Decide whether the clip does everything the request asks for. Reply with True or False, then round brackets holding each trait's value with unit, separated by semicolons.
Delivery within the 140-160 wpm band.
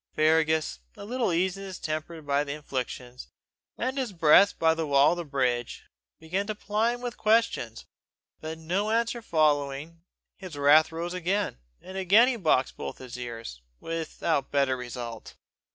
False (170 wpm)